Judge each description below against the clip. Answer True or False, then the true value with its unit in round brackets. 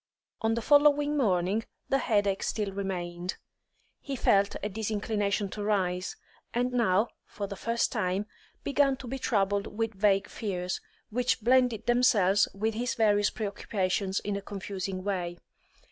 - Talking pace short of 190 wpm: True (145 wpm)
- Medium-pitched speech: False (205 Hz)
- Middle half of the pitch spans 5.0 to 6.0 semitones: False (3.2 semitones)